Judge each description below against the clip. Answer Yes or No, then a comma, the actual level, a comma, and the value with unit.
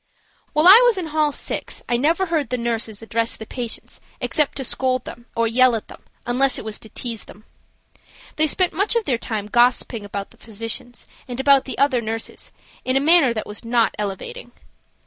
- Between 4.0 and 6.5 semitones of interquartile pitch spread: Yes, average, 4.4 semitones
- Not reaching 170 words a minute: No, average, 195 wpm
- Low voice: No, high, 245 Hz